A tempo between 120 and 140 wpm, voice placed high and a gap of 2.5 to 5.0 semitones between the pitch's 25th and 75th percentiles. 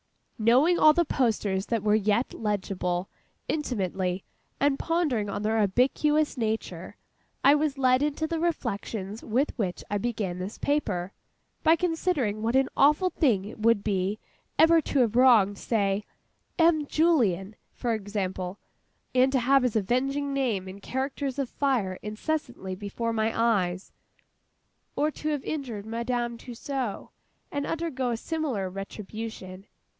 No: slow, 135 wpm; high, 235 Hz; wide, 5.6 semitones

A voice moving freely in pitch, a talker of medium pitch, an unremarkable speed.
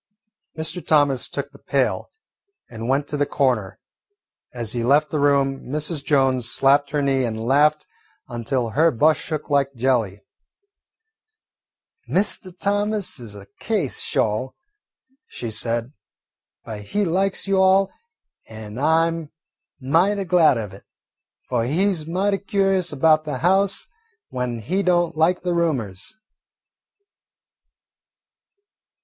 No: wide, 6.1 semitones; medium, 145 Hz; slow, 130 wpm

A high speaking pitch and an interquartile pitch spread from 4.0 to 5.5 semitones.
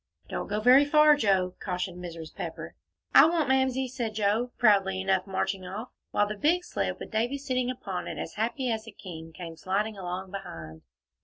Yes: high, 210 Hz; average, 5.2 semitones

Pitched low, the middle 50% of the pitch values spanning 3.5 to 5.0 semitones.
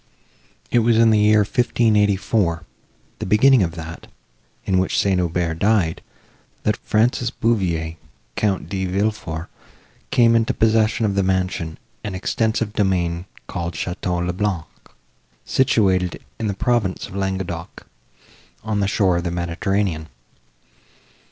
Yes: very low, 95 Hz; average, 3.9 semitones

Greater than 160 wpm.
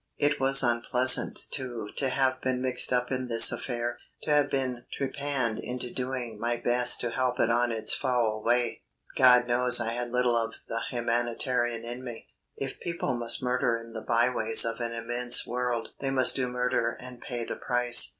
Yes: average, 190 wpm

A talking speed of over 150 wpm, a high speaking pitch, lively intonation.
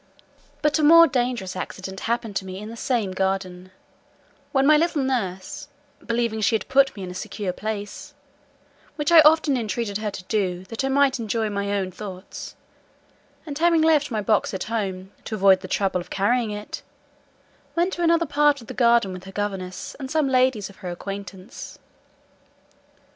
Yes: average, 180 wpm; high, 220 Hz; wide, 5.8 semitones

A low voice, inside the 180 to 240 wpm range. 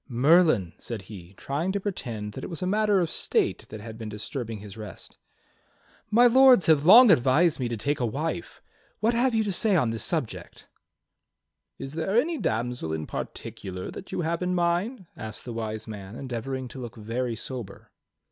Yes: low, 130 Hz; average, 185 wpm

